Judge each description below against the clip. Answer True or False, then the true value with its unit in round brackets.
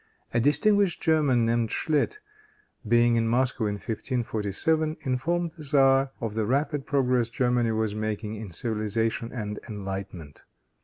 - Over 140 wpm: False (135 wpm)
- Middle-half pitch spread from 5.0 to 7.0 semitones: False (4.2 semitones)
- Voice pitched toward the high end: False (120 Hz)